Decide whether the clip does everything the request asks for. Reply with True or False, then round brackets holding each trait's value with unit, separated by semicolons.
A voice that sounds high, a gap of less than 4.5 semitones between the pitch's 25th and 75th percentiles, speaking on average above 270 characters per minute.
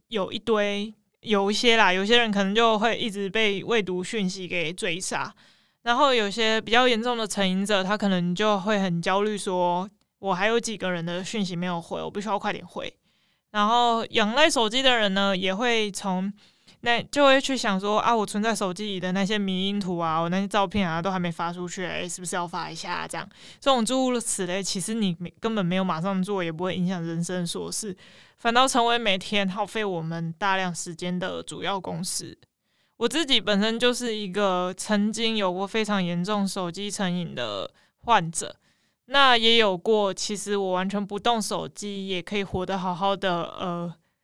True (200 Hz; 3.1 semitones; 285 characters per minute)